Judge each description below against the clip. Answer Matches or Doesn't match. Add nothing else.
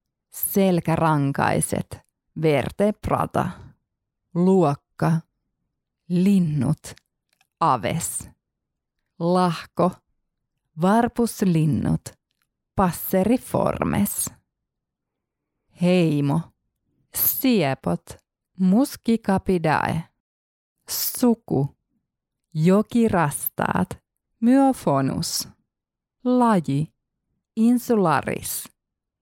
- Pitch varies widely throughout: Matches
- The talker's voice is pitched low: Doesn't match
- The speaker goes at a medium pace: Doesn't match